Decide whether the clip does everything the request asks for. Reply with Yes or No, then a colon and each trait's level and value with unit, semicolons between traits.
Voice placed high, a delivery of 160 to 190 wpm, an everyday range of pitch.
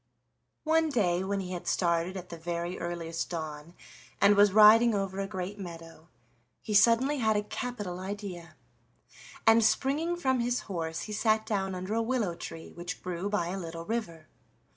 Yes: high, 195 Hz; average, 170 wpm; average, 4.2 semitones